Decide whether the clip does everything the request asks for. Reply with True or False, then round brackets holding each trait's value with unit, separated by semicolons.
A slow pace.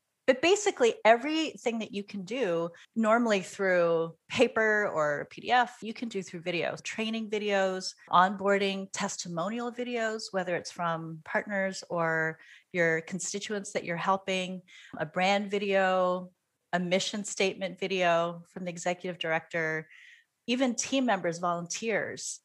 True (125 wpm)